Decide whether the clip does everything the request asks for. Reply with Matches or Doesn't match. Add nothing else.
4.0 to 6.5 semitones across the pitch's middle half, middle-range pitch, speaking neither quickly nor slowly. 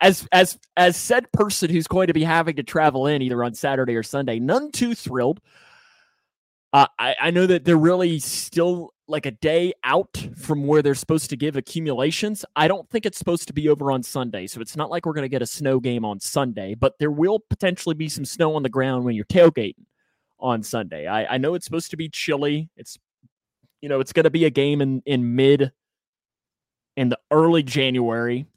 Doesn't match